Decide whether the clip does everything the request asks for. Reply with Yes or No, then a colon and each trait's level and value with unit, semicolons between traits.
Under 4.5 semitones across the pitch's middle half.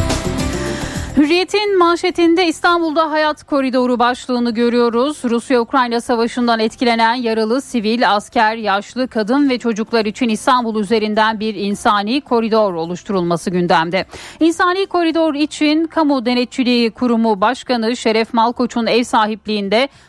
Yes: average, 4.1 semitones